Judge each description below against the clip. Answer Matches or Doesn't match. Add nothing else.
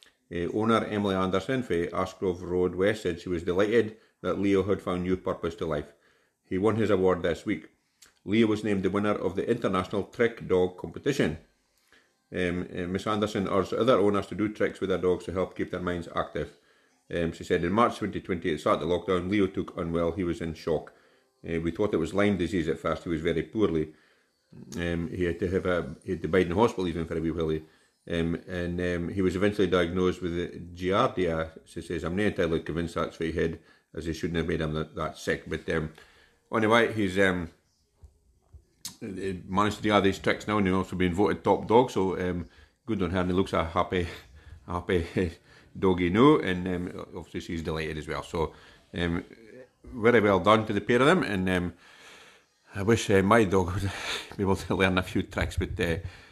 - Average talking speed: Doesn't match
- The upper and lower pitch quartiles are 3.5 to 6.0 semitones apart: Doesn't match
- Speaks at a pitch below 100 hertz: Matches